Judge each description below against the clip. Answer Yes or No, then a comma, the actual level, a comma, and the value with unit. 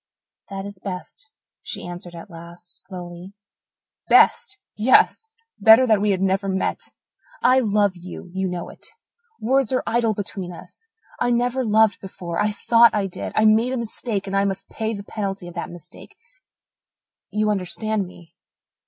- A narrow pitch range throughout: No, average, 3.4 semitones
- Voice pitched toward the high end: Yes, high, 200 Hz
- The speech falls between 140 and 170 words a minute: Yes, average, 160 wpm